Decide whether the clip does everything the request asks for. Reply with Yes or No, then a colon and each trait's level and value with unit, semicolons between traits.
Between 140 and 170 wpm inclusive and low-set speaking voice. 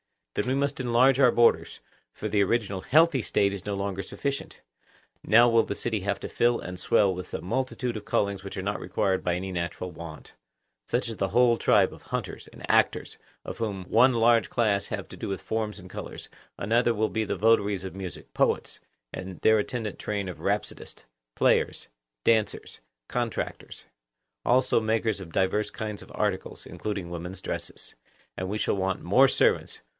No: average, 180 wpm; low, 105 Hz